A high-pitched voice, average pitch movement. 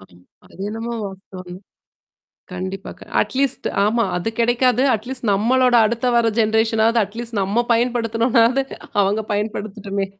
Yes: high, 225 Hz; average, 3.3 semitones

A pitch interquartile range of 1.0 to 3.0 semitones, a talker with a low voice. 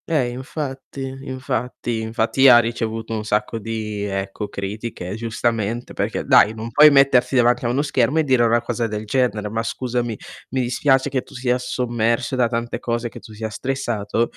Yes: narrow, 2.5 semitones; low, 120 Hz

